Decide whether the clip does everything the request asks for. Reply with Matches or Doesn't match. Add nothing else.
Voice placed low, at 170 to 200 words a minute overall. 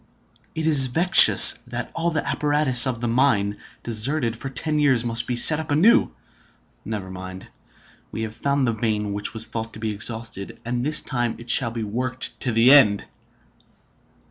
Matches